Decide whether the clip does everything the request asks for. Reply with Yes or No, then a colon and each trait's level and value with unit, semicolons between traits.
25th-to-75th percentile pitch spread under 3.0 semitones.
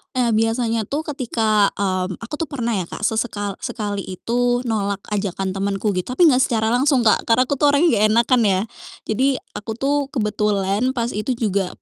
No: average, 3.7 semitones